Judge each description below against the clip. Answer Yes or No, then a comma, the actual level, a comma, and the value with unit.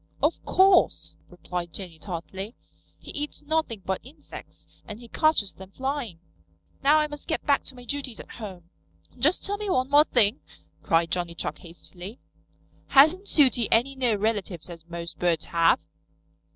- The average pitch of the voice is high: Yes, high, 225 Hz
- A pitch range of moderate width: No, wide, 8.4 semitones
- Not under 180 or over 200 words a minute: No, average, 160 wpm